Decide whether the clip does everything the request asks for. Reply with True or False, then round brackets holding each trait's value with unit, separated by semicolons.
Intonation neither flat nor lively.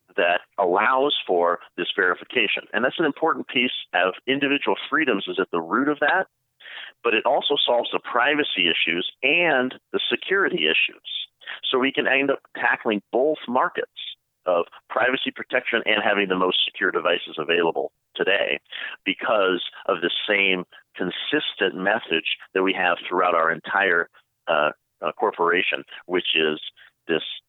False (6.4 semitones)